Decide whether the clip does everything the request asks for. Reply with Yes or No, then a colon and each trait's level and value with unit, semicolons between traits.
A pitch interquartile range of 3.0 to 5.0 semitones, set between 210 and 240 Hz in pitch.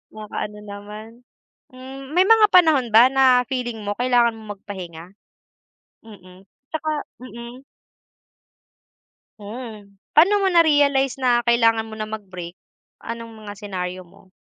Yes: average, 4.3 semitones; high, 230 Hz